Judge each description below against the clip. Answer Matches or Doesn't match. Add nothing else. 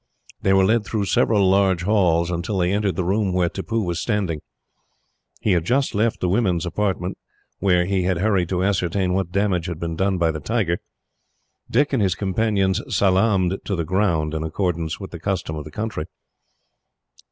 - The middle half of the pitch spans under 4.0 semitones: Matches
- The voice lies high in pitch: Doesn't match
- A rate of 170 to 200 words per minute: Matches